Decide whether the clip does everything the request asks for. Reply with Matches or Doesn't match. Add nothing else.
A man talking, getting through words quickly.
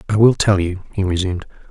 Matches